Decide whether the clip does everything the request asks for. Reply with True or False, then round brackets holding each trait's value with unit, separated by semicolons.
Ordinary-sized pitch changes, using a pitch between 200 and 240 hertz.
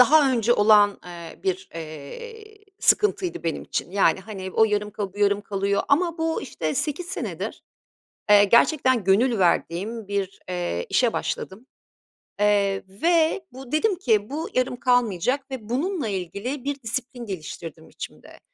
False (6.1 semitones; 220 Hz)